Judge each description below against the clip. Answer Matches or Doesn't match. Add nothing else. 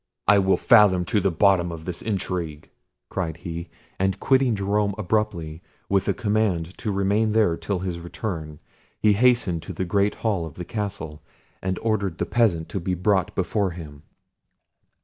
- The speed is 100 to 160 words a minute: Doesn't match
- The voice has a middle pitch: Doesn't match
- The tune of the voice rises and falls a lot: Doesn't match